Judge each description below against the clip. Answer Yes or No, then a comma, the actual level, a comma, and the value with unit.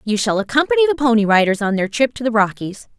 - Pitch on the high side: Yes, high, 230 Hz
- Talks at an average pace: No, fast, 240 wpm